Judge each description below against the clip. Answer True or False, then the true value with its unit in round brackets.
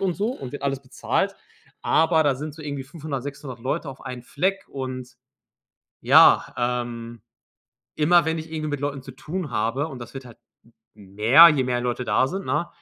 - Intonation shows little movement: False (4.0 semitones)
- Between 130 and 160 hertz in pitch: True (135 Hz)